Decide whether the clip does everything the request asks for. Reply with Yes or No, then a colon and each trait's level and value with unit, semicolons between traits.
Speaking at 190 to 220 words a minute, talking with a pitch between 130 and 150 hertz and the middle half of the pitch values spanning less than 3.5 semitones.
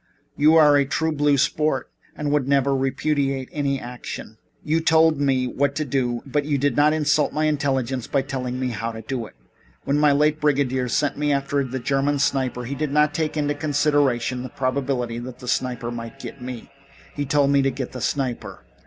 Yes: average, 195 wpm; medium, 140 Hz; narrow, 2.4 semitones